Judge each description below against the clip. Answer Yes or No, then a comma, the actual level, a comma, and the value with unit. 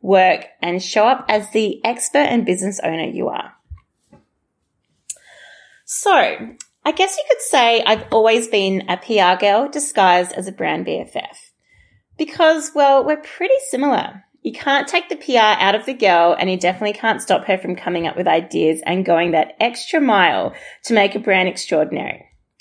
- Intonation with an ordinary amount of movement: No, wide, 7.2 semitones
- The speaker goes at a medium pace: Yes, average, 170 wpm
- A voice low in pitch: No, high, 215 Hz